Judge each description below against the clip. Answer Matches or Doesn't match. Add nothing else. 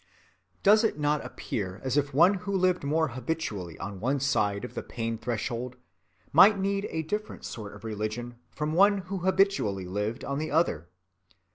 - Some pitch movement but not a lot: Doesn't match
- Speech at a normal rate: Matches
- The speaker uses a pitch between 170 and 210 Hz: Doesn't match